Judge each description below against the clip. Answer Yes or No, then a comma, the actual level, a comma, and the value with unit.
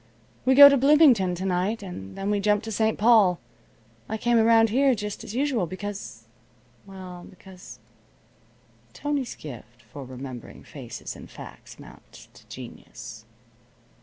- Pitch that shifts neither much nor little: No, wide, 6.6 semitones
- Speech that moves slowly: No, average, 145 wpm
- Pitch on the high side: Yes, high, 200 Hz